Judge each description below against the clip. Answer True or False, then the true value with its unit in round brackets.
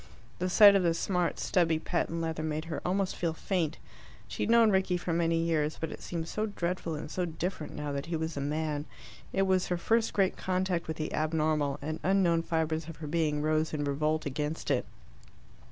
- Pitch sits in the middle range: True (165 Hz)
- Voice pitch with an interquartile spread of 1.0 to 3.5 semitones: True (2.6 semitones)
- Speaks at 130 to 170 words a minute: False (205 wpm)